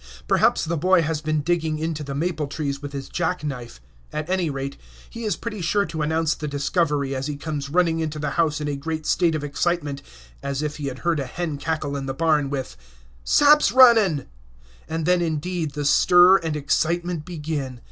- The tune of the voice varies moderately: Yes, average, 3.1 semitones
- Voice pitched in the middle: Yes, medium, 155 Hz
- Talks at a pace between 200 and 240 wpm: Yes, fast, 205 wpm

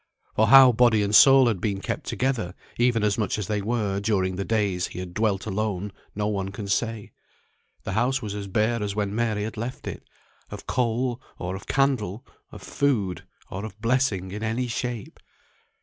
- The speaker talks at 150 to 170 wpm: No, average, 185 wpm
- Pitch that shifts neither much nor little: Yes, average, 3.1 semitones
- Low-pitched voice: Yes, low, 105 Hz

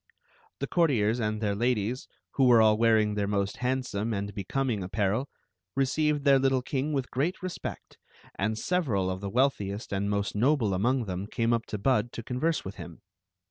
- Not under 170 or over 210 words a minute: Yes, average, 190 wpm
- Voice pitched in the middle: No, low, 115 Hz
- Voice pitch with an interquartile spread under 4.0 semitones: No, average, 4.7 semitones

